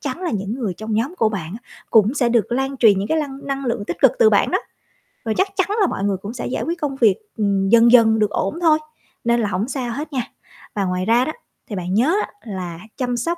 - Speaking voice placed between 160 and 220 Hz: No, high, 235 Hz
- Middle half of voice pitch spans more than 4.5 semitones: Yes, average, 5.1 semitones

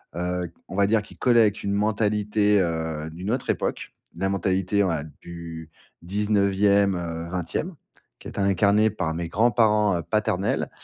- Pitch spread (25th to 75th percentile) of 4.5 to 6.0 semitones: No, average, 3.3 semitones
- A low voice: Yes, low, 100 Hz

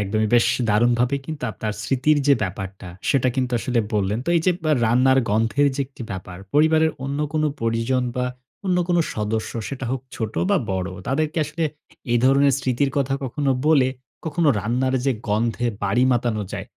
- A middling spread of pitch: Yes, average, 4.2 semitones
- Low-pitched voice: Yes, low, 125 Hz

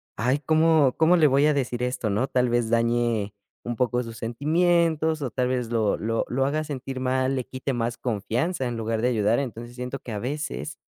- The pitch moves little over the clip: No, average, 3.5 semitones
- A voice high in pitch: No, low, 125 Hz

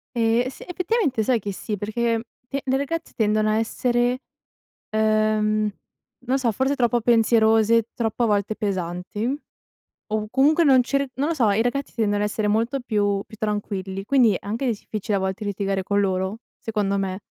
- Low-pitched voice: No, high, 220 Hz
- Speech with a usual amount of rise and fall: Yes, average, 3.2 semitones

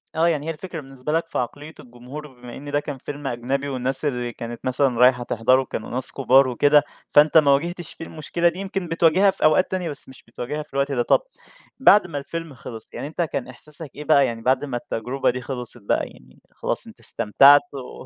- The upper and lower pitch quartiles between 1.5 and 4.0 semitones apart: Yes, average, 3.7 semitones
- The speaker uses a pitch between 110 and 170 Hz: Yes, medium, 140 Hz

